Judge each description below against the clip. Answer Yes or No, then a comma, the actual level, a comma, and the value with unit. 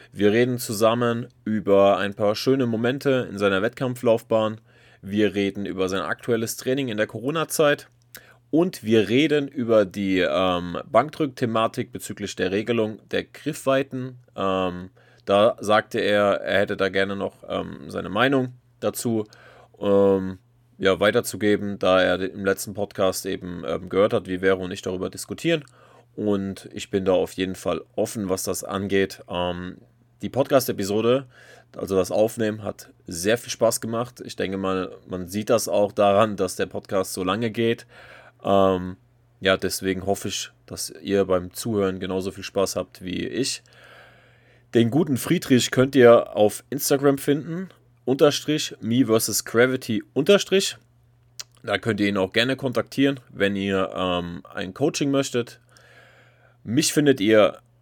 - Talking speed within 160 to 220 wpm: No, average, 150 wpm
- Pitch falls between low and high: No, low, 110 Hz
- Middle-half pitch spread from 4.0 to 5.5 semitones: Yes, average, 4.4 semitones